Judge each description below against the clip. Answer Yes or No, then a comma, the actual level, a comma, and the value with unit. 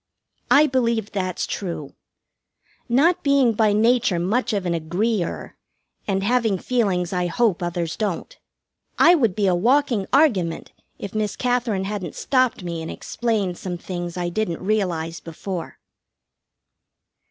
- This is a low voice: No, high, 200 Hz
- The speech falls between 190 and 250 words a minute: No, average, 140 wpm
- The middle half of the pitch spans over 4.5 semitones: Yes, average, 5.1 semitones